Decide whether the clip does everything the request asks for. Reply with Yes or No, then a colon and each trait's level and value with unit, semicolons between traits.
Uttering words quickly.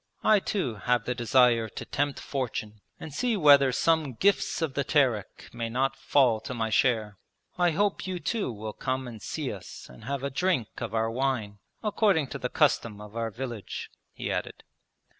No: average, 185 wpm